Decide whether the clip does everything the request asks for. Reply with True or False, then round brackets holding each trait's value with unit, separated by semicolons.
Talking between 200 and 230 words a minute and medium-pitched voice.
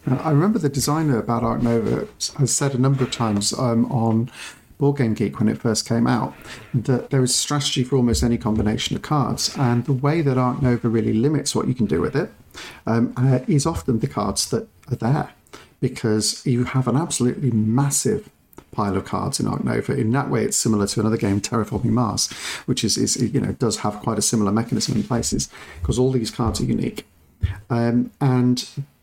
False (205 wpm; 120 Hz)